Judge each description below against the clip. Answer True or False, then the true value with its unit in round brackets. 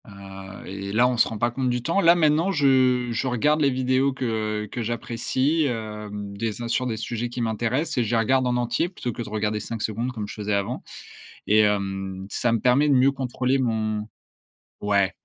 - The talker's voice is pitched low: True (120 Hz)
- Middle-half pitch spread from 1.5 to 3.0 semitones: False (3.4 semitones)